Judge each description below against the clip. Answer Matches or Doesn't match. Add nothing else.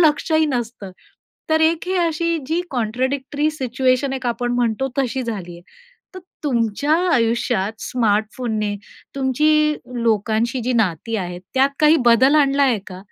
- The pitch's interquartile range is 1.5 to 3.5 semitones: Doesn't match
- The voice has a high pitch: Matches